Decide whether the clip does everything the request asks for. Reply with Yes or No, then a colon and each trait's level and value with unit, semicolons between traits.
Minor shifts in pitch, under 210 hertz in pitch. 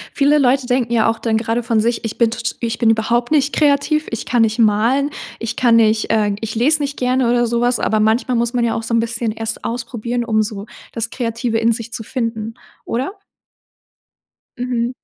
No: narrow, 1.7 semitones; high, 235 Hz